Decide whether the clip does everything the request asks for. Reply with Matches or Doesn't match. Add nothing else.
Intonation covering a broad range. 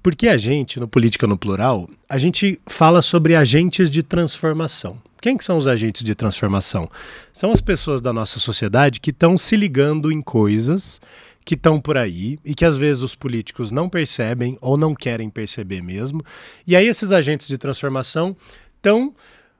Matches